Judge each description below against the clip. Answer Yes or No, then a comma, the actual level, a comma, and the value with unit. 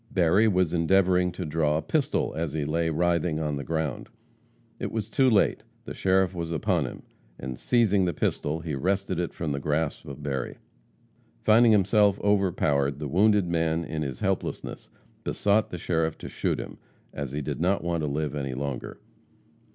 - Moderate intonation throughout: Yes, average, 4.2 semitones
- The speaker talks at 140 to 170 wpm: No, average, 180 wpm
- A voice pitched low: Yes, very low, 85 Hz